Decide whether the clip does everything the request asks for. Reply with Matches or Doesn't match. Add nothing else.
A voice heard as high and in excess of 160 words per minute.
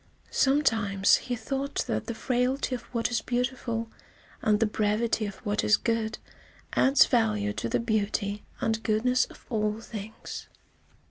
Doesn't match